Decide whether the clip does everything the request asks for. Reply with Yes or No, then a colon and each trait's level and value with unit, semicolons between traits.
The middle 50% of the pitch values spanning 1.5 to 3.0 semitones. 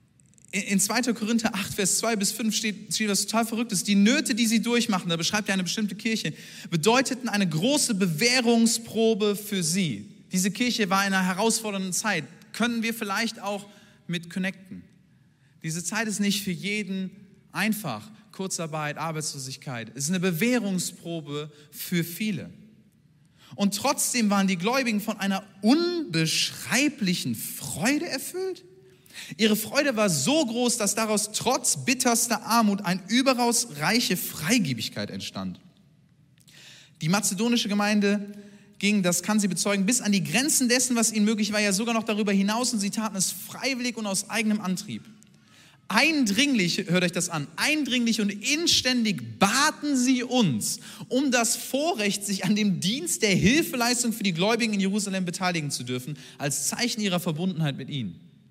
No: average, 4.2 semitones